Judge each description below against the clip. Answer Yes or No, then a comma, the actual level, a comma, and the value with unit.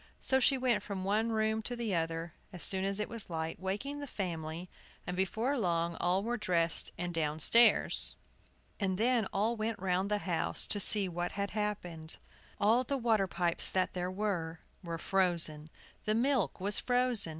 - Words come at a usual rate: Yes, average, 175 wpm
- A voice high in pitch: Yes, high, 195 Hz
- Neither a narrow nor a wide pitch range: Yes, average, 4.2 semitones